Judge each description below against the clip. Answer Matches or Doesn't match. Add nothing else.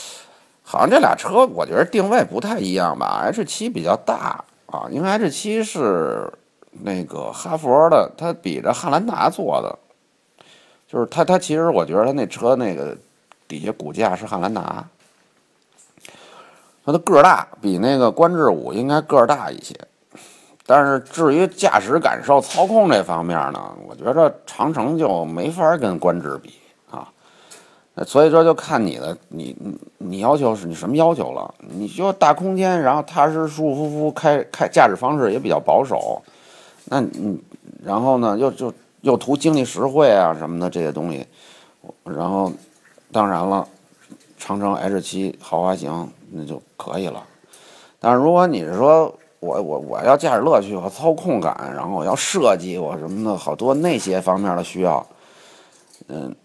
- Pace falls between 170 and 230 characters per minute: Doesn't match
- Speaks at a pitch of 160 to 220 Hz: Doesn't match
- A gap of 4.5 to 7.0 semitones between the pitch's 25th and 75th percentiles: Doesn't match